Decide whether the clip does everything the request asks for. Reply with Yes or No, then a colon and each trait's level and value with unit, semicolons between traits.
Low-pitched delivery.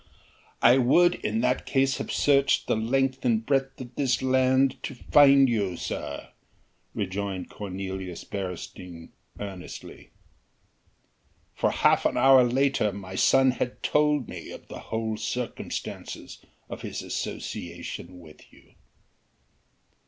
Yes: low, 125 Hz